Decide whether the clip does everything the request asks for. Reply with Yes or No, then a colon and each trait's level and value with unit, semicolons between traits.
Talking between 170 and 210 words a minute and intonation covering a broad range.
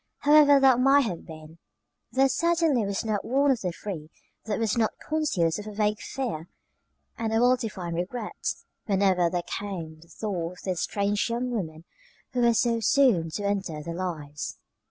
Yes: average, 175 wpm; wide, 6.1 semitones